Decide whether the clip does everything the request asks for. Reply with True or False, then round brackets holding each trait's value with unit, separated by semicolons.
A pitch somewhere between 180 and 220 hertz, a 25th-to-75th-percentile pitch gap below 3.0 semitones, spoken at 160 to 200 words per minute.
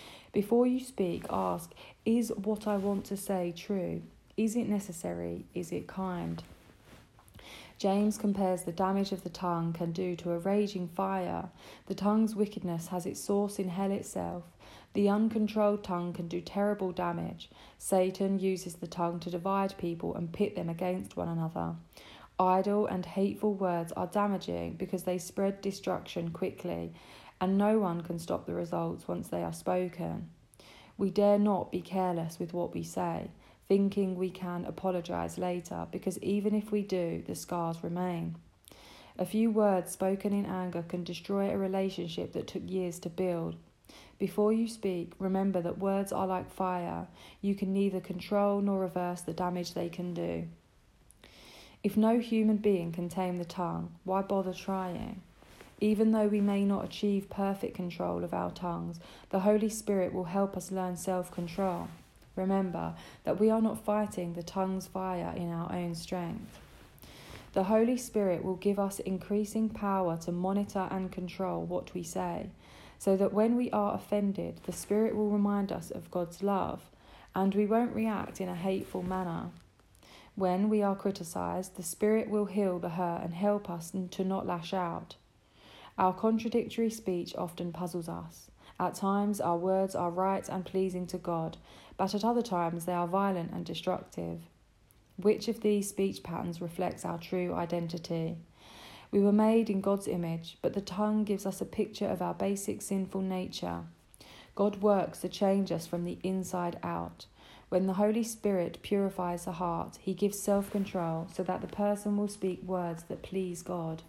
True (185 Hz; 2.6 semitones; 165 wpm)